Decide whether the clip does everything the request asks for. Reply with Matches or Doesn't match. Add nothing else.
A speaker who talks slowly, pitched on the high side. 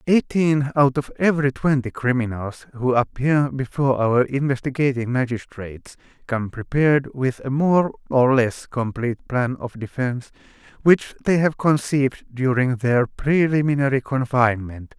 Doesn't match